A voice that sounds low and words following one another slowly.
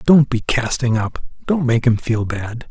No: low, 120 Hz; average, 200 wpm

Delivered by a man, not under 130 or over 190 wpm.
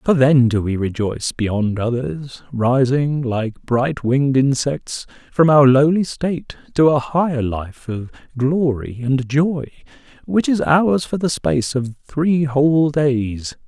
Yes: male; average, 150 wpm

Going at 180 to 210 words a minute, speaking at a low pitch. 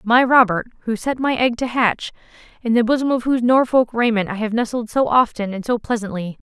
No: average, 195 wpm; high, 230 Hz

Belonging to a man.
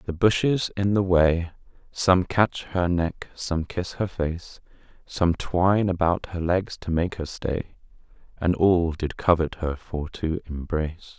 Yes: male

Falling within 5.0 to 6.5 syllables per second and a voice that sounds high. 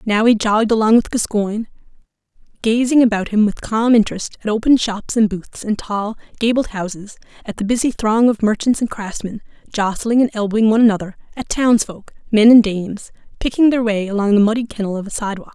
Yes: 5.9 syllables/s; high, 220 Hz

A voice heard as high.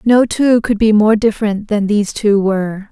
Yes: high, 210 Hz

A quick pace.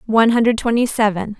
No: average, 170 wpm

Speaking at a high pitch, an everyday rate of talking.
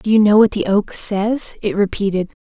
No: high, 205 Hz; fast, 220 wpm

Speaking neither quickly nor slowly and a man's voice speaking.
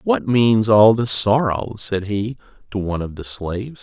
Yes: average, 190 wpm; male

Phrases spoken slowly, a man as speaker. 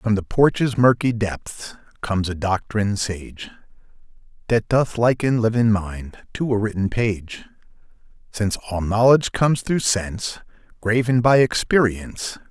Yes: slow, 130 wpm; male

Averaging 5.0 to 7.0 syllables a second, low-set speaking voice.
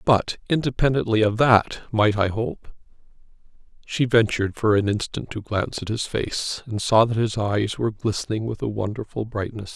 Yes: 5.1 syllables/s; low, 110 Hz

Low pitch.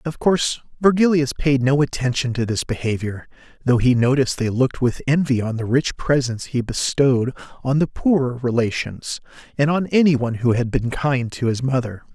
Yes: low, 130 Hz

